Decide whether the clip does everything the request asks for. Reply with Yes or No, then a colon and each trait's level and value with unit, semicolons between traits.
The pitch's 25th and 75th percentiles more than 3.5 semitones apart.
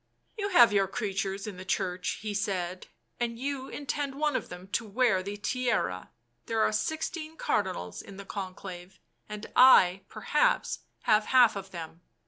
Yes: average, 5.2 semitones